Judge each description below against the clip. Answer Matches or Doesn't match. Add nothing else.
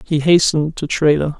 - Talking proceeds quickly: Doesn't match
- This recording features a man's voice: Matches